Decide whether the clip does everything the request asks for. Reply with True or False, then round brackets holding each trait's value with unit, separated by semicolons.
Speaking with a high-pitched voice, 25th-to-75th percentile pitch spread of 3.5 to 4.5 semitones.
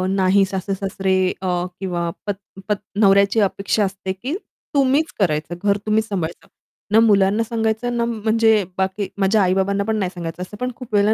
False (200 Hz; 2.6 semitones)